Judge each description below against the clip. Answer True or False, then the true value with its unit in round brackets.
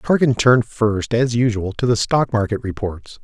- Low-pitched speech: True (115 Hz)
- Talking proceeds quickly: False (185 wpm)